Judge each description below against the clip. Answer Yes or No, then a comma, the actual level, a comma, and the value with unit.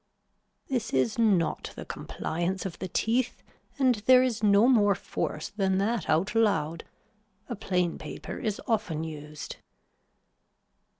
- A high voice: Yes, high, 200 Hz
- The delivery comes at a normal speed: No, slow, 130 wpm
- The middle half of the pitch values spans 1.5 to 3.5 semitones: No, wide, 5.4 semitones